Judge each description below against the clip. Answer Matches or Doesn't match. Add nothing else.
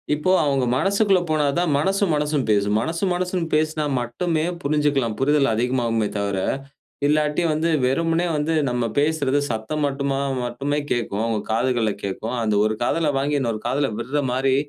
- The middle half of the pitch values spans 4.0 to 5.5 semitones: Matches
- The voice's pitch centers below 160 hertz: Matches